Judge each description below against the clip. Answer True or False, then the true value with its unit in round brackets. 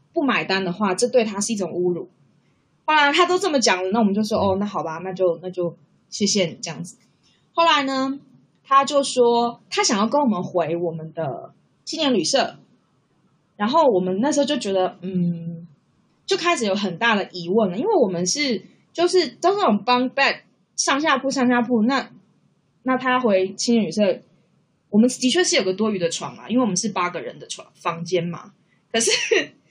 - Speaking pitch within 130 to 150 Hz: False (215 Hz)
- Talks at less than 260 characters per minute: False (280 characters per minute)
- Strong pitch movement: True (6.6 semitones)